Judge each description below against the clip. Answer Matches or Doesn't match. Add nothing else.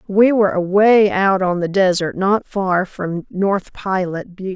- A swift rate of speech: Doesn't match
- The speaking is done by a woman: Matches